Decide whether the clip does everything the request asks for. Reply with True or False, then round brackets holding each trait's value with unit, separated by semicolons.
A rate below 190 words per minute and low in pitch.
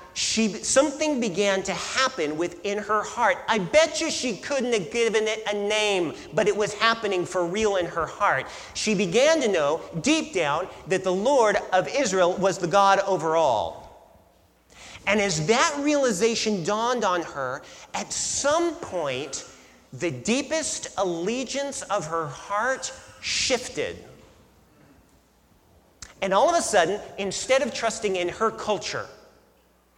False (140 wpm; 210 Hz)